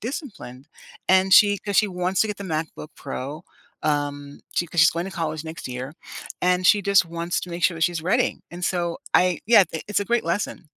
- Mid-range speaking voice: Yes, medium, 175 Hz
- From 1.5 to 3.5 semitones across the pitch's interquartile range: No, average, 3.9 semitones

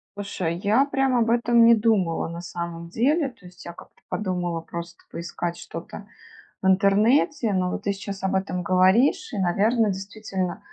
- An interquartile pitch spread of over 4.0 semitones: Yes, average, 4.5 semitones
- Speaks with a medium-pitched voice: No, high, 195 Hz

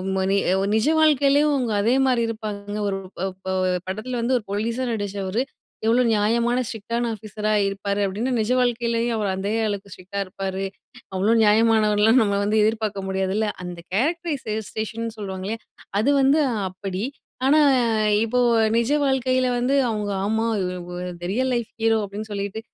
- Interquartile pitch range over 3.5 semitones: No, average, 3.1 semitones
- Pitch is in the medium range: No, high, 220 Hz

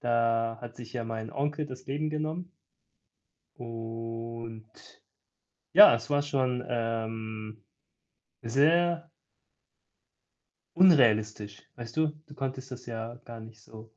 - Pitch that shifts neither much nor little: Yes, average, 3.6 semitones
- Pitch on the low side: Yes, low, 115 Hz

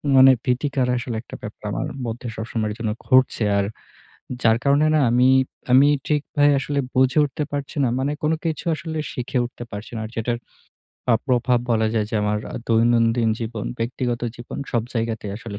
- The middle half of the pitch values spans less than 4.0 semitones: Yes, average, 3.0 semitones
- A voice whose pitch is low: Yes, low, 120 Hz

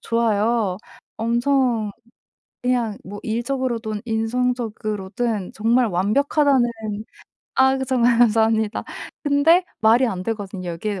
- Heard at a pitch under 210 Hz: No, high, 230 Hz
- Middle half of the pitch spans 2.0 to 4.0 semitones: Yes, average, 2.9 semitones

